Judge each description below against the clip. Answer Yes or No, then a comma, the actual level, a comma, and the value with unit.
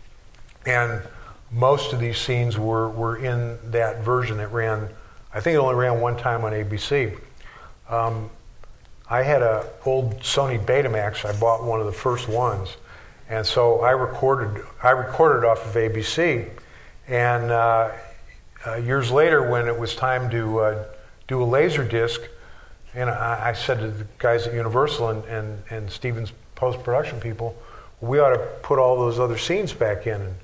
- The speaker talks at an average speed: Yes, average, 170 wpm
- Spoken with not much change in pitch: Yes, narrow, 2.0 semitones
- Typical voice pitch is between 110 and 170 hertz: Yes, low, 115 Hz